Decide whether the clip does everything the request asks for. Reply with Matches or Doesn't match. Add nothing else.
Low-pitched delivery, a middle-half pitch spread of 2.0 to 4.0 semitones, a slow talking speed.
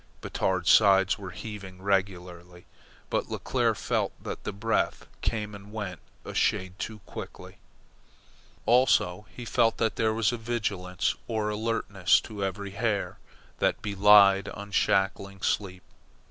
Matches